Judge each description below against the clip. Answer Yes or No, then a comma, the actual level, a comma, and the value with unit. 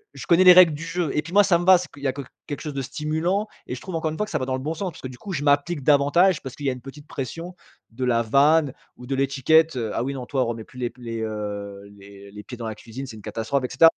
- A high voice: No, medium, 140 Hz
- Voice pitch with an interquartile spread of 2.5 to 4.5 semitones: No, average, 4.9 semitones